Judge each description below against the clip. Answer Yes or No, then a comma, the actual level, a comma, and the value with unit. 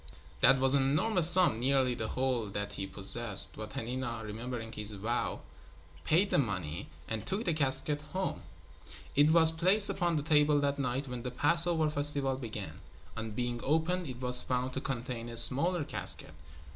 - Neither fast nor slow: Yes, average, 170 wpm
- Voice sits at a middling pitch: No, low, 130 Hz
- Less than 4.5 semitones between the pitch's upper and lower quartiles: No, average, 4.8 semitones